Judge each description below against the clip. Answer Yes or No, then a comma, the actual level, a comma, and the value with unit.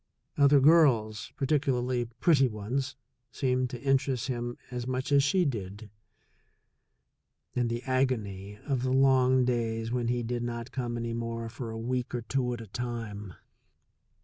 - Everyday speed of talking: Yes, average, 150 wpm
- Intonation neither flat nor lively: No, narrow, 2.2 semitones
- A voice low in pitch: Yes, low, 120 Hz